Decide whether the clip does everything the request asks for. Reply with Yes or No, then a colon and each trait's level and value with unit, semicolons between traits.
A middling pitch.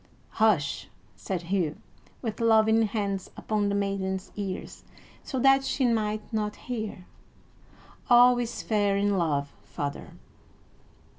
No: high, 210 Hz